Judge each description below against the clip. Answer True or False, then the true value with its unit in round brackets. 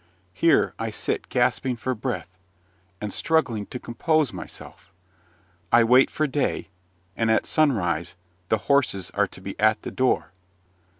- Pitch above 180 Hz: False (120 Hz)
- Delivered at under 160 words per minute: True (140 wpm)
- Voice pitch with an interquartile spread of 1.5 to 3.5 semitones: False (4.2 semitones)